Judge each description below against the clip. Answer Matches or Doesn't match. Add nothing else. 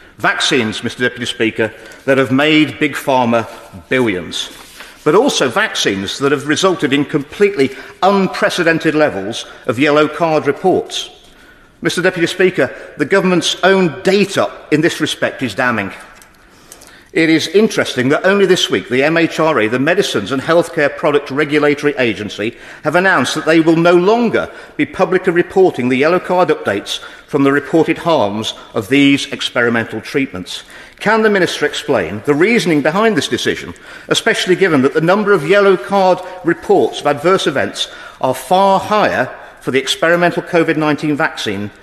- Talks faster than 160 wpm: Doesn't match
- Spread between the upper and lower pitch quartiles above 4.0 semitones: Matches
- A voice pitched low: Doesn't match